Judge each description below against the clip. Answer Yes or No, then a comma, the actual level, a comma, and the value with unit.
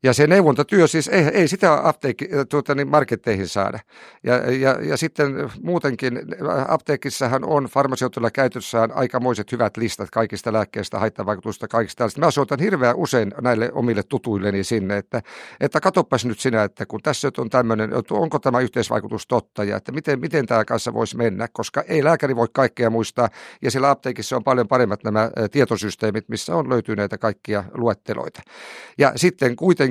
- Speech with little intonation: No, average, 4.0 semitones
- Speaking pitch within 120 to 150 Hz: Yes, low, 125 Hz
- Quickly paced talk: Yes, fast, 160 wpm